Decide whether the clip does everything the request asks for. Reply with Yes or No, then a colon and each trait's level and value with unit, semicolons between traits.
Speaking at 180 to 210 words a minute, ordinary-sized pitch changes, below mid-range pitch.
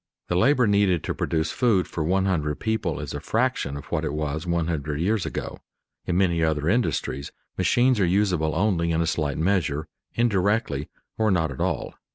Yes: average, 190 wpm; average, 4.7 semitones; very low, 85 Hz